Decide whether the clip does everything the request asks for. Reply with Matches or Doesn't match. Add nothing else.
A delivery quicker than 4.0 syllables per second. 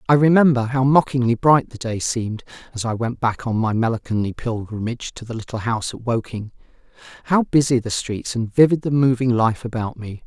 Matches